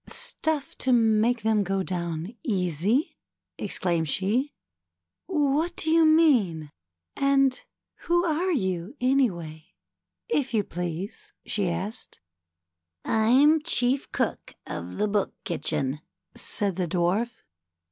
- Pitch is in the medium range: No, high, 220 Hz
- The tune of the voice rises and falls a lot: Yes, wide, 7.8 semitones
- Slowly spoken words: Yes, slow, 125 wpm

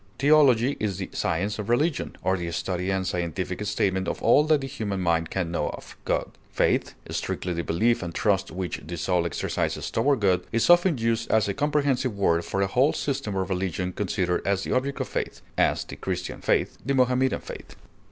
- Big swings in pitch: Yes, wide, 5.8 semitones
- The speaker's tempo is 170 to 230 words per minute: Yes, average, 200 wpm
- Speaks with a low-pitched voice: Yes, low, 100 Hz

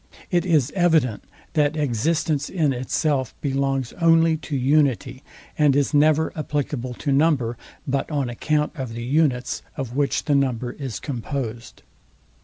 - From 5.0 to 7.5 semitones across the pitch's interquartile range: No, average, 3.2 semitones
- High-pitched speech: No, medium, 140 Hz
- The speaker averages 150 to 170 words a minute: No, average, 140 wpm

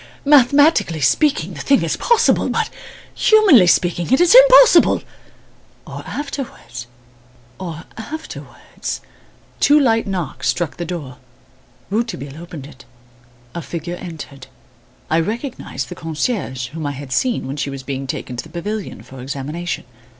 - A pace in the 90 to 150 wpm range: Yes, average, 140 wpm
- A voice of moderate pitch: Yes, medium, 175 Hz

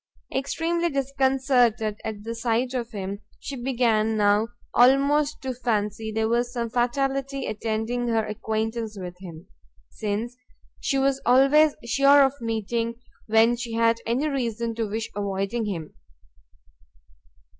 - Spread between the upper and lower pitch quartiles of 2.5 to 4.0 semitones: Yes, average, 3.4 semitones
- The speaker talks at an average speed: No, slow, 130 wpm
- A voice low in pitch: No, high, 235 Hz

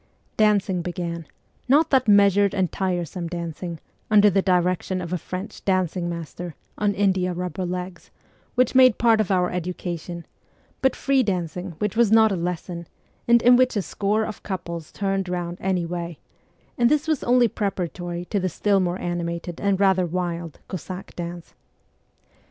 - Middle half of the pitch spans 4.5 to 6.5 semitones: No, average, 2.8 semitones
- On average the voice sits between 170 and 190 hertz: Yes, medium, 185 Hz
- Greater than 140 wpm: Yes, average, 165 wpm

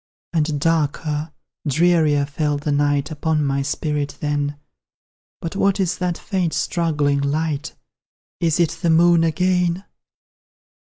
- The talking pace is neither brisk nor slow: No, slow, 120 wpm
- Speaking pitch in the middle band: Yes, medium, 155 Hz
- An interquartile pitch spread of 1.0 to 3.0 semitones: Yes, average, 2.7 semitones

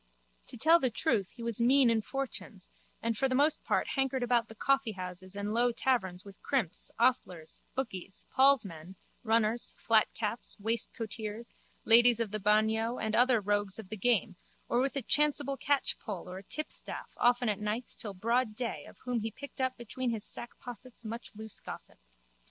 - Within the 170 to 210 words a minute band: Yes, average, 175 wpm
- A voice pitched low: No, high, 230 Hz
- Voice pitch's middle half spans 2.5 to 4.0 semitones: Yes, average, 3.4 semitones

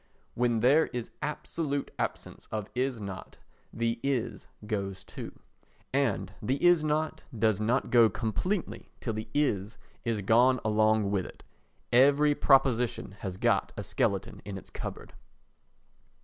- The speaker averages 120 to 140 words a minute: Yes, slow, 135 wpm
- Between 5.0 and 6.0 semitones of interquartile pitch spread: No, average, 4.5 semitones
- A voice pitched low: Yes, low, 115 Hz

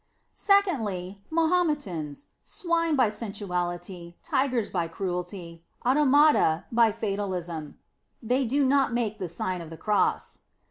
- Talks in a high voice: Yes, high, 205 Hz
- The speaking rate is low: Yes, slow, 125 wpm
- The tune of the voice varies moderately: No, wide, 7.5 semitones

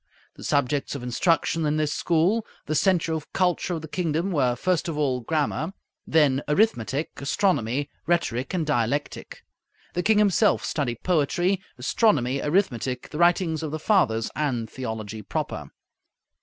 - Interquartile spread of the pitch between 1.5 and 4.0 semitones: No, average, 5.0 semitones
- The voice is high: No, medium, 155 Hz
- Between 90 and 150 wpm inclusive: Yes, average, 145 wpm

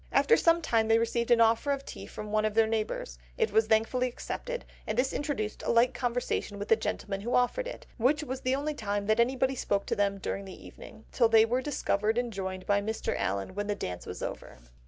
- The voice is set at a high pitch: Yes, high, 225 Hz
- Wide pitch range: No, average, 3.6 semitones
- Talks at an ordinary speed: No, fast, 230 wpm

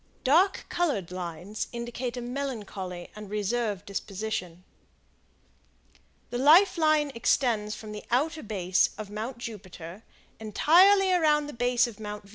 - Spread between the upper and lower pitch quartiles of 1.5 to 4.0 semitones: No, wide, 5.6 semitones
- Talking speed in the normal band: No, slow, 130 wpm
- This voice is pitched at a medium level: No, high, 225 Hz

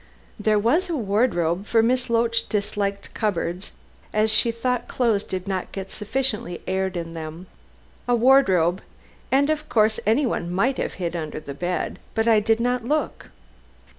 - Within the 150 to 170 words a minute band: Yes, average, 160 wpm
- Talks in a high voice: Yes, high, 215 Hz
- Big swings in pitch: No, average, 4.5 semitones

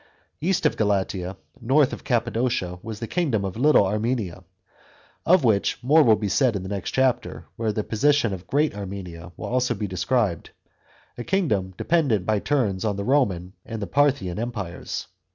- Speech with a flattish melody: No, average, 5.2 semitones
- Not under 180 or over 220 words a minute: No, average, 170 wpm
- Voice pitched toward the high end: No, low, 110 Hz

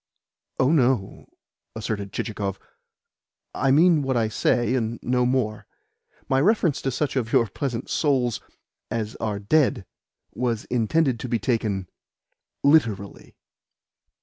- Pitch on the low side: Yes, low, 120 Hz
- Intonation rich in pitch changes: No, average, 3.6 semitones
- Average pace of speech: No, slow, 120 wpm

